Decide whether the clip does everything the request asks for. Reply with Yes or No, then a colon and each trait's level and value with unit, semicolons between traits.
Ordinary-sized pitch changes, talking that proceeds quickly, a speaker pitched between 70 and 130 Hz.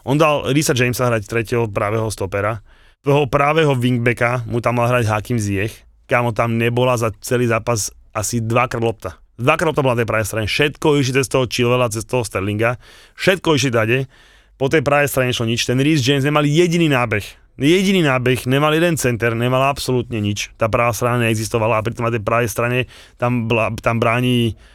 Yes: average, 3.0 semitones; fast, 190 wpm; low, 120 Hz